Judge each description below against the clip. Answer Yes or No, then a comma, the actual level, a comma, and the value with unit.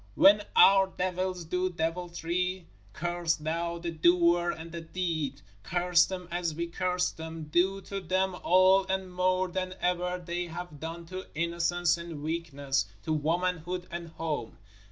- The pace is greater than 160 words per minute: No, average, 150 wpm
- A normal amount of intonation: No, narrow, 1.8 semitones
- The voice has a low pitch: No, medium, 175 Hz